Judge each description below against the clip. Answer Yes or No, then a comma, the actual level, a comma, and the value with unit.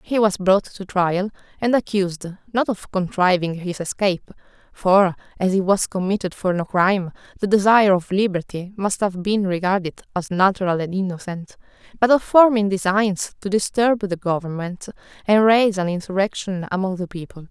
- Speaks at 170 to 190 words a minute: No, average, 160 wpm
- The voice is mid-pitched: No, high, 195 Hz